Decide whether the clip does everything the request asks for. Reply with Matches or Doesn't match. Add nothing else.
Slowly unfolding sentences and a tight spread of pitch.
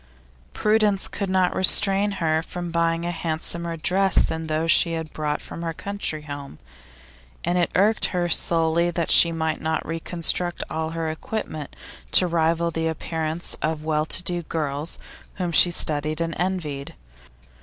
Doesn't match